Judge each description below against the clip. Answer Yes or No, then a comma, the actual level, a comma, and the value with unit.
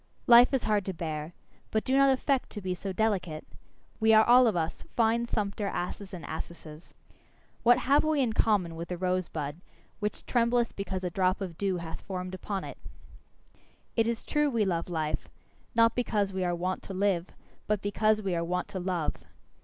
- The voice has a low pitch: No, high, 195 Hz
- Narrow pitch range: No, average, 4.3 semitones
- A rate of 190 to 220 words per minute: Yes, average, 195 wpm